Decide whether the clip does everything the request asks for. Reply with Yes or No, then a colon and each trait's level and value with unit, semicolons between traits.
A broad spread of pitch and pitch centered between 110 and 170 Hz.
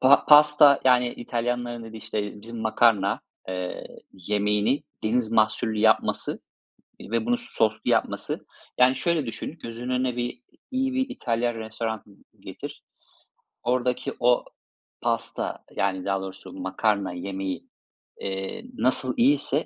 No: average, 3.3 semitones; low, 115 Hz